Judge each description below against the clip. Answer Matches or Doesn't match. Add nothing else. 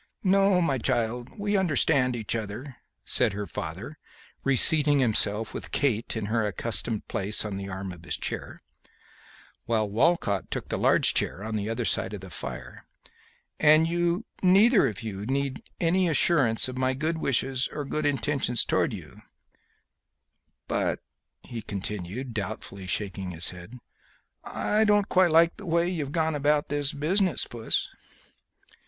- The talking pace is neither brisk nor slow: Matches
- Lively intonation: Matches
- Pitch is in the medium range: Doesn't match